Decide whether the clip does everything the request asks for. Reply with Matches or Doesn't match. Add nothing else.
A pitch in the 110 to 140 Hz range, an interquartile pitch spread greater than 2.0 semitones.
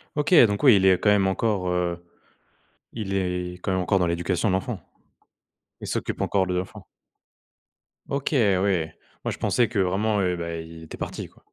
Doesn't match